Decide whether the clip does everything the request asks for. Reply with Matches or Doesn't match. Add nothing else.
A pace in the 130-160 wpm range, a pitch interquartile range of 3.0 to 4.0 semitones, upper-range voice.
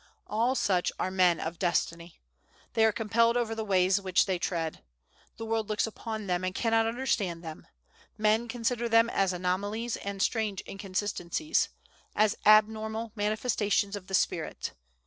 Matches